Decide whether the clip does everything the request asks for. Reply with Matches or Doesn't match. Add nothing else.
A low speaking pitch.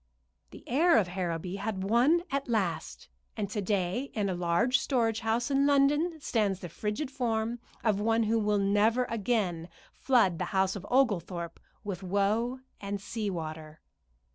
Doesn't match